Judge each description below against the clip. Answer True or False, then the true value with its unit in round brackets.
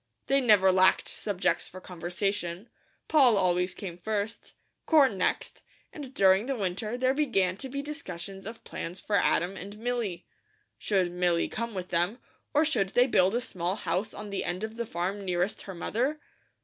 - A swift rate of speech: False (175 wpm)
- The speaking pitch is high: True (200 Hz)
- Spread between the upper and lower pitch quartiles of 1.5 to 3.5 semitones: False (4.6 semitones)